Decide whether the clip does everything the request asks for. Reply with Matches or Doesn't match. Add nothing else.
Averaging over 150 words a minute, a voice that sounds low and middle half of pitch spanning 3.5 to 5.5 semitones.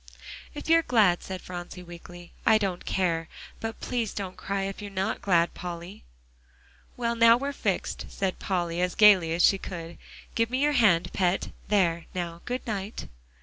Doesn't match